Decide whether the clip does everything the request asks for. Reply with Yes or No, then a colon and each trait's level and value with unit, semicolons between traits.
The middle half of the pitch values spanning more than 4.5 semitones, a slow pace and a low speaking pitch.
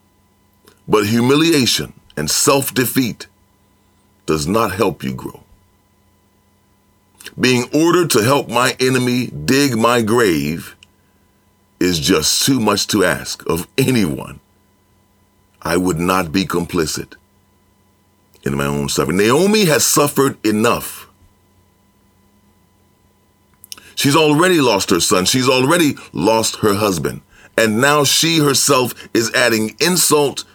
No: average, 4.1 semitones; slow, 110 wpm; low, 100 Hz